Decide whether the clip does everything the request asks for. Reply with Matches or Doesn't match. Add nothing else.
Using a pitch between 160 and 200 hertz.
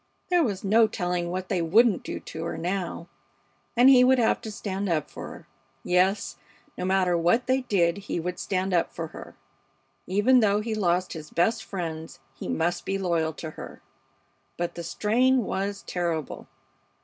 Matches